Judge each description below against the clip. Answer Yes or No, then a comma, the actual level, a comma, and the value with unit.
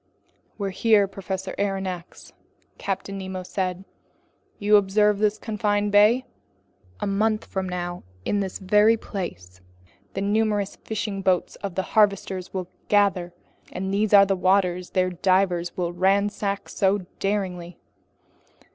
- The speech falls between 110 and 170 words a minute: Yes, slow, 135 wpm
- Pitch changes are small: Yes, narrow, 1.9 semitones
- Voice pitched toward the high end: Yes, high, 195 Hz